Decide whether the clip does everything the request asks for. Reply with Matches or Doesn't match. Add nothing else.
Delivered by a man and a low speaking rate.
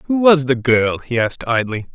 Doesn't match